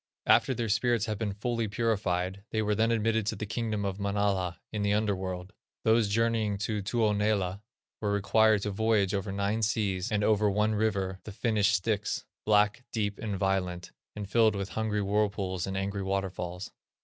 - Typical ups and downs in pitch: No, narrow, 2.1 semitones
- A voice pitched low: Yes, low, 105 Hz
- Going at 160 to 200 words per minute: Yes, average, 175 wpm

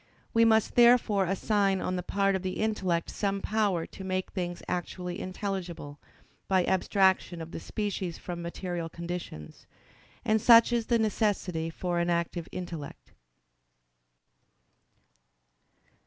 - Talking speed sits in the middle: No, slow, 125 wpm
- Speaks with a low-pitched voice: No, medium, 185 Hz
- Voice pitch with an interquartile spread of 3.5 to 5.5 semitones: No, average, 3.1 semitones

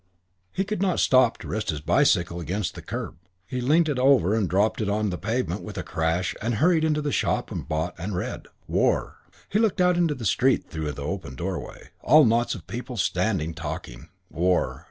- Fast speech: Yes, fast, 210 wpm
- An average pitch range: No, wide, 8.1 semitones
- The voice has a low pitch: Yes, low, 110 Hz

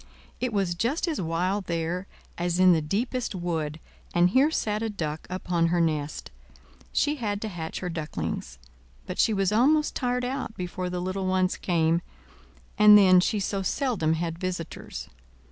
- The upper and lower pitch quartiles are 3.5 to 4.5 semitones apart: Yes, average, 4.1 semitones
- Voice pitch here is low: No, medium, 185 Hz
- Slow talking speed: No, average, 165 wpm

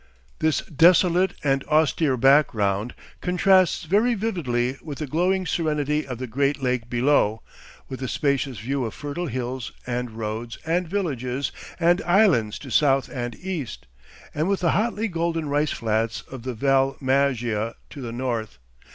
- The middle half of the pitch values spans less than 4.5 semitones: No, wide, 5.4 semitones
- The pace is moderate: Yes, average, 150 wpm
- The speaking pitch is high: No, medium, 140 Hz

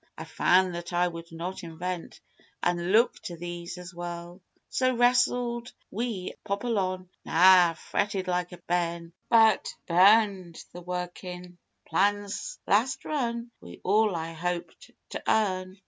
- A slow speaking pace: Yes, slow, 130 wpm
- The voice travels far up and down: No, average, 3.5 semitones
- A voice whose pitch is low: No, medium, 185 Hz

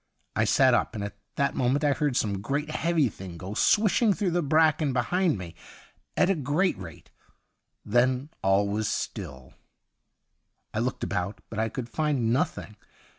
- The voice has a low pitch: Yes, low, 125 Hz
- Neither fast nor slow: Yes, average, 165 wpm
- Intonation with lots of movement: Yes, wide, 7.1 semitones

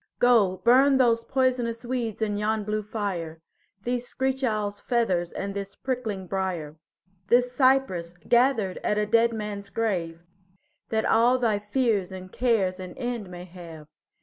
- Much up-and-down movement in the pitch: No, average, 4.3 semitones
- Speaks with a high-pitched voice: Yes, high, 215 Hz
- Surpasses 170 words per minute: No, average, 150 wpm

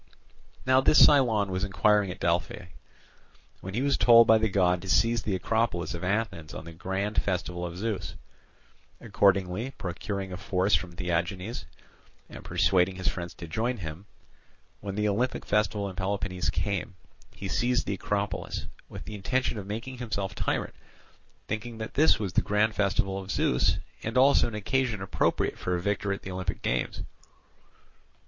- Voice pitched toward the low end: Yes, low, 100 Hz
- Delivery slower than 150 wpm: No, average, 165 wpm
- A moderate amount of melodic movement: Yes, average, 3.3 semitones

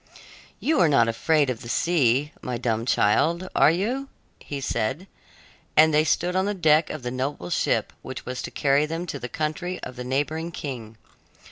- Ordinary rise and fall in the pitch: Yes, average, 4.7 semitones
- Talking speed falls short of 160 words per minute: No, average, 190 wpm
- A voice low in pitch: No, medium, 145 Hz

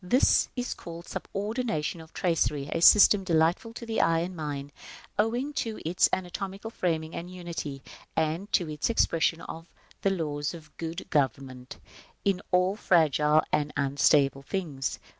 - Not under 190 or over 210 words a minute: No, average, 150 wpm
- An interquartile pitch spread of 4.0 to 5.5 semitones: Yes, average, 4.3 semitones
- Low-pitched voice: No, medium, 165 Hz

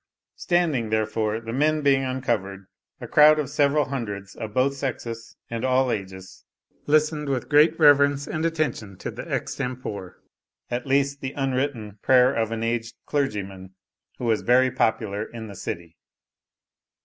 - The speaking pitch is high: No, low, 125 Hz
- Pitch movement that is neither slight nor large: Yes, average, 4.5 semitones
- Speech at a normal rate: Yes, average, 150 wpm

